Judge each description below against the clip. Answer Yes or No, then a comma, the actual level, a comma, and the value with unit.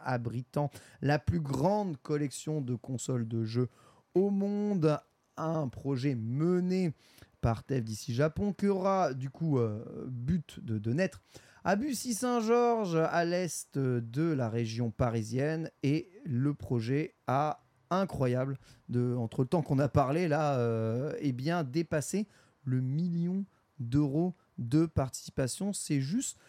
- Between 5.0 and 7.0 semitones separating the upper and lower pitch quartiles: Yes, wide, 5.4 semitones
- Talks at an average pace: No, slow, 130 wpm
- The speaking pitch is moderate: Yes, medium, 145 Hz